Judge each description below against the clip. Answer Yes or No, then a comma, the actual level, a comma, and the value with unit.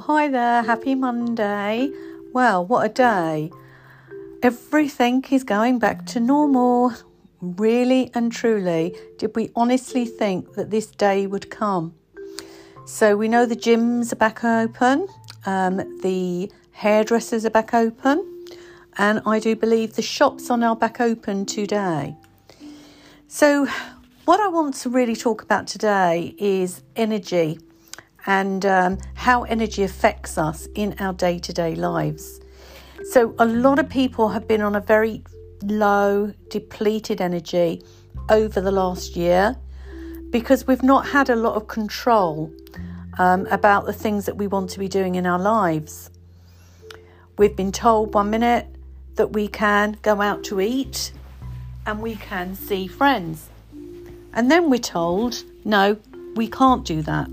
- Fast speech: No, average, 145 wpm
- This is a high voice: Yes, high, 210 Hz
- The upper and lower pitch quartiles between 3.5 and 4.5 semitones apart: No, average, 5.0 semitones